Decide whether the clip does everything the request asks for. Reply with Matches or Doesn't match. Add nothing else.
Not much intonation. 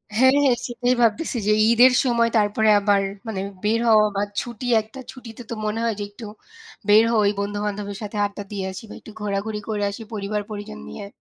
Matches